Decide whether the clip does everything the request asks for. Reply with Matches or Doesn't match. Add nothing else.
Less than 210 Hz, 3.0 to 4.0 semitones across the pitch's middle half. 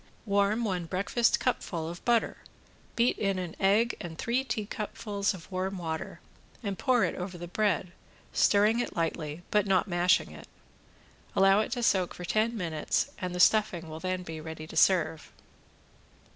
Matches